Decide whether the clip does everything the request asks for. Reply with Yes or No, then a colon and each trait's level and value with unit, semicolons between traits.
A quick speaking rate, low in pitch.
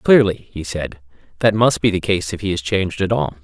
Yes: fast, 245 wpm; very low, 95 Hz